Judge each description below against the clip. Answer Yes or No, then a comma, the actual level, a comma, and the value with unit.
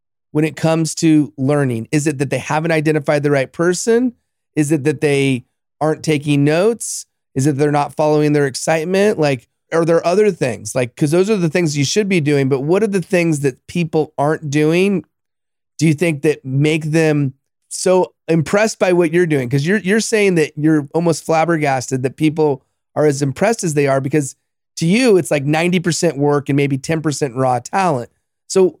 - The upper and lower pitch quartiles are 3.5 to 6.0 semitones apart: No, average, 2.9 semitones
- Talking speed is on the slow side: No, average, 195 wpm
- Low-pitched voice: No, medium, 155 Hz